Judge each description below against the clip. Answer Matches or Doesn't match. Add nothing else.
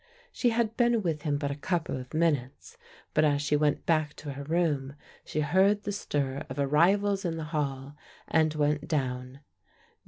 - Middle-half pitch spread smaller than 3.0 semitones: Doesn't match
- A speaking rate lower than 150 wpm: Doesn't match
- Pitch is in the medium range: Matches